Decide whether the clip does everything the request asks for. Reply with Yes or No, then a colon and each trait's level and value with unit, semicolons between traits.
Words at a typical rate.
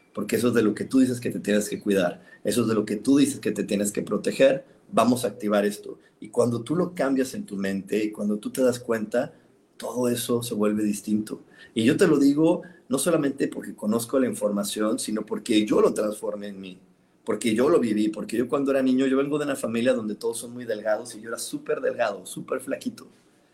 No: fast, 235 wpm